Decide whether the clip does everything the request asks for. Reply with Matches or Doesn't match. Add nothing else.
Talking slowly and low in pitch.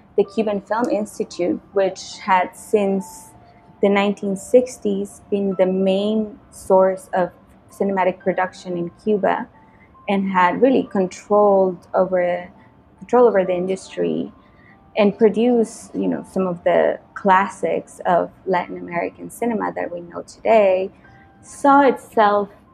Doesn't match